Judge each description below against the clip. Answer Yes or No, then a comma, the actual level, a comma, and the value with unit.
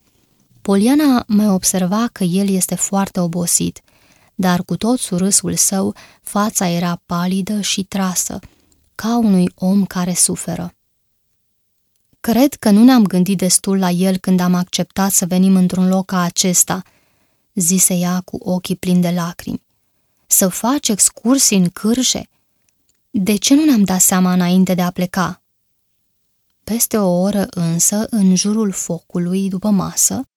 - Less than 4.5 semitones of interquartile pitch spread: Yes, narrow, 2.5 semitones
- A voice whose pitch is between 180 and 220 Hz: Yes, medium, 185 Hz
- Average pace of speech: Yes, average, 140 wpm